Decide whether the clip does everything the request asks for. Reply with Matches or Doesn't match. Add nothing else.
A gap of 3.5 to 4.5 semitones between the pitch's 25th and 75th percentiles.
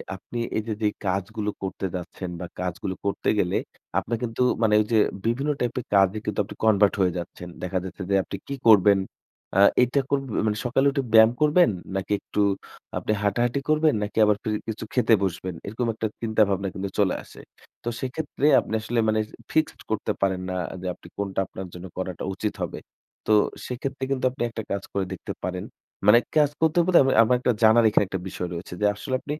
Matches